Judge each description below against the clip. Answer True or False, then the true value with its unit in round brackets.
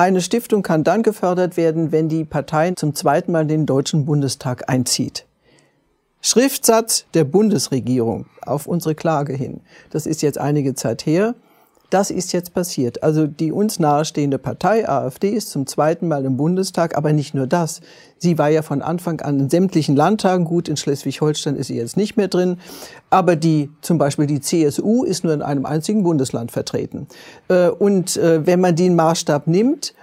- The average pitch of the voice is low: False (160 Hz)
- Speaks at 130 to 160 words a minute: False (175 wpm)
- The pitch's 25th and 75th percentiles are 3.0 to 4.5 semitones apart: True (3.9 semitones)